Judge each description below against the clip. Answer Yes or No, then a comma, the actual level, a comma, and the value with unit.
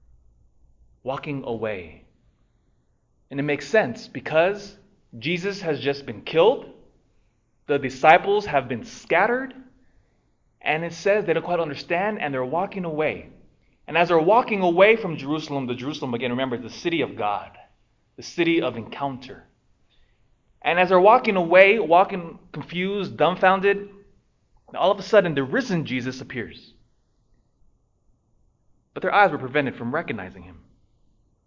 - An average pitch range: No, wide, 7.4 semitones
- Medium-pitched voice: Yes, medium, 155 Hz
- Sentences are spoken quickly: No, slow, 135 wpm